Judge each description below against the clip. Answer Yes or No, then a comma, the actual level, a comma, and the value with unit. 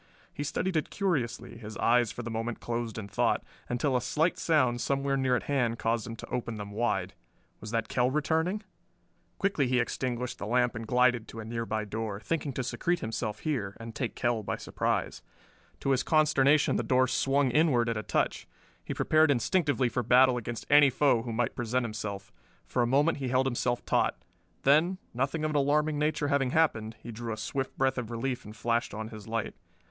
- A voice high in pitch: No, low, 125 Hz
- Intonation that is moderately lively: Yes, average, 3.7 semitones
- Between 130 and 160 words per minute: No, average, 200 wpm